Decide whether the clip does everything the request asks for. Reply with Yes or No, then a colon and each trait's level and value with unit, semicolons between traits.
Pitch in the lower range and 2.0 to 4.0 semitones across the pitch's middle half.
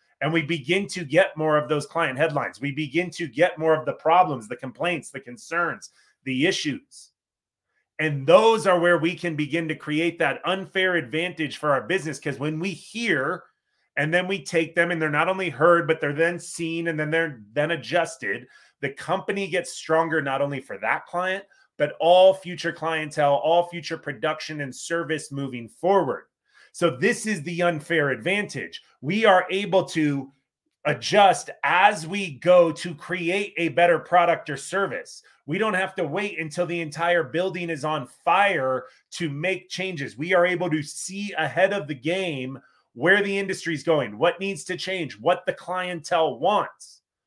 No: medium, 170 Hz; average, 3.0 semitones